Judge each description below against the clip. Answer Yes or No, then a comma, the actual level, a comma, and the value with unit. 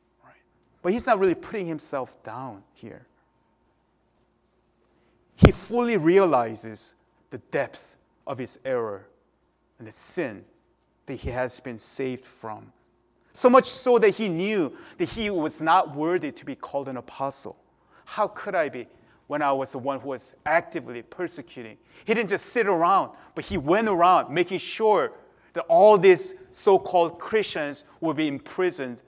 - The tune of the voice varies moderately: No, wide, 8.7 semitones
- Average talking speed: Yes, average, 150 wpm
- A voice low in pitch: No, medium, 165 Hz